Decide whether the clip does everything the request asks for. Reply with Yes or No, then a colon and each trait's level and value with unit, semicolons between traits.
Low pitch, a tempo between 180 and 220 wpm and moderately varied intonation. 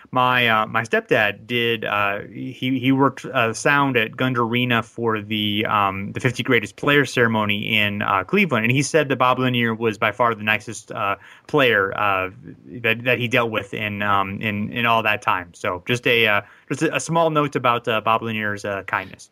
Yes: low, 115 Hz; average, 200 wpm; average, 3.1 semitones